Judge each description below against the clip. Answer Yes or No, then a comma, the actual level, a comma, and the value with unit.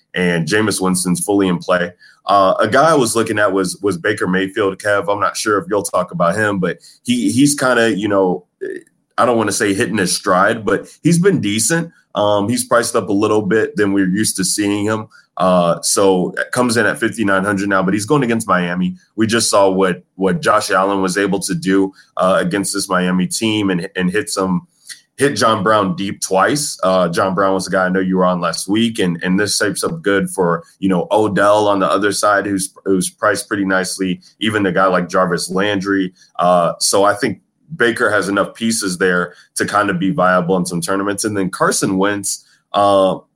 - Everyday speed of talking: No, fast, 215 wpm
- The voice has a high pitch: No, very low, 95 Hz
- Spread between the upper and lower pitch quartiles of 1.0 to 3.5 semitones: Yes, narrow, 2.4 semitones